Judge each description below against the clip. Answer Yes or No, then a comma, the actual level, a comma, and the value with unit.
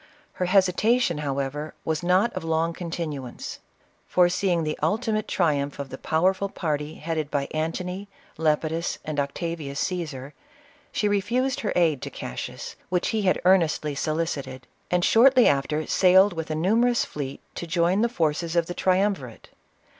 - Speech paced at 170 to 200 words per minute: No, average, 150 wpm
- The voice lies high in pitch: No, medium, 165 Hz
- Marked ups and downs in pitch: No, average, 3.8 semitones